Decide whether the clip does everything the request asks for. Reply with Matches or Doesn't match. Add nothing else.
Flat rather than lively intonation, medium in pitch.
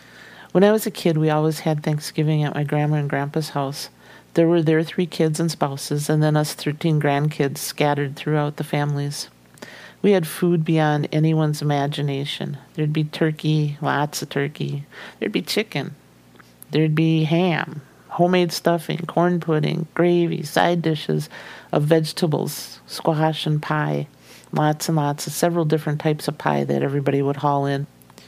Matches